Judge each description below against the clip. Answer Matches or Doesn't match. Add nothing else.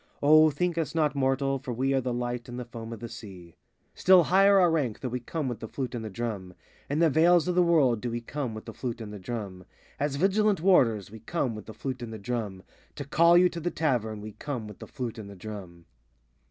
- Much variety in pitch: Matches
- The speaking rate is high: Matches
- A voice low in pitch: Matches